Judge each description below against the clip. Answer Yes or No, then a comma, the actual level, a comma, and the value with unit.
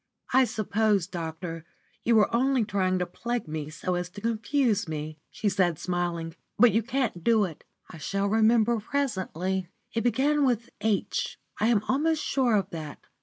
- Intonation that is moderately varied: Yes, average, 5.0 semitones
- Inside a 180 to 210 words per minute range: No, average, 170 wpm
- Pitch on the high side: Yes, high, 205 Hz